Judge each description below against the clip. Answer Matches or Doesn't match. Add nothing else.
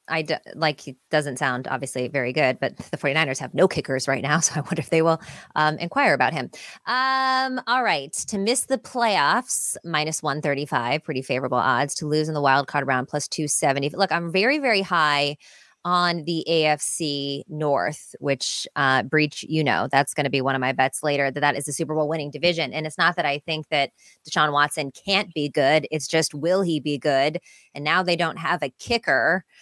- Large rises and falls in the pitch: Doesn't match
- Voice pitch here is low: Doesn't match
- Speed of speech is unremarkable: Doesn't match